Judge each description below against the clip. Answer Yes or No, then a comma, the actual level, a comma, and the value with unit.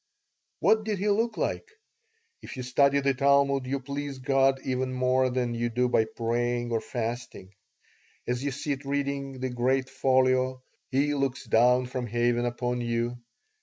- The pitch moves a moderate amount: No, narrow, 2.2 semitones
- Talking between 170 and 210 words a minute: No, average, 160 wpm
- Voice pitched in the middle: No, low, 130 Hz